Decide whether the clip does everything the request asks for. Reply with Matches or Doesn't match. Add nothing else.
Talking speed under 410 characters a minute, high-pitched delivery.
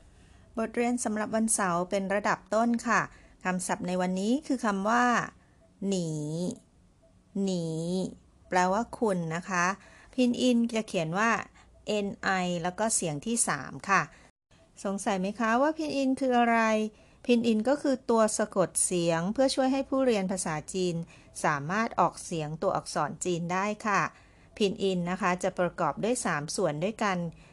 Doesn't match